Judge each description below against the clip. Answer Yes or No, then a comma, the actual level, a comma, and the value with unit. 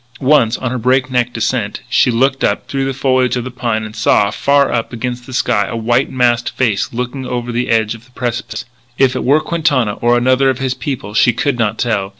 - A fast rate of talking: Yes, fast, 230 wpm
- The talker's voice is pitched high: No, low, 125 Hz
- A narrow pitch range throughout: Yes, narrow, 2.1 semitones